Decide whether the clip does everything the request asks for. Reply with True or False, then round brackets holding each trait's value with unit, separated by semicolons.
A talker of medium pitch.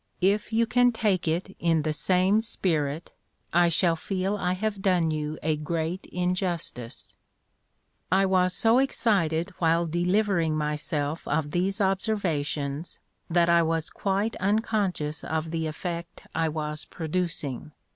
True (170 Hz)